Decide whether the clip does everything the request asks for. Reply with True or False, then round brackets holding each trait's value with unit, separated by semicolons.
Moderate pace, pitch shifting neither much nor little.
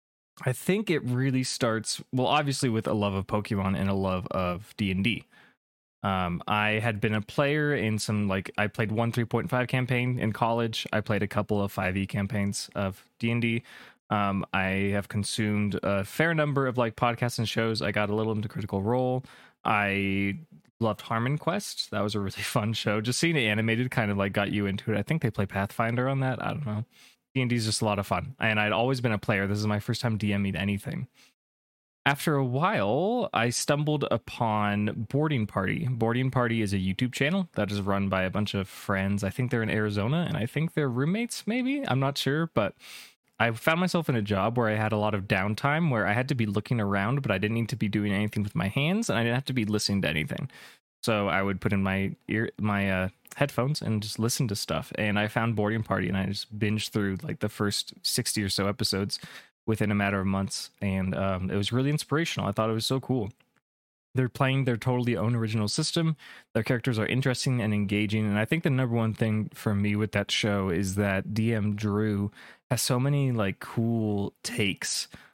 False (215 wpm; 3.9 semitones)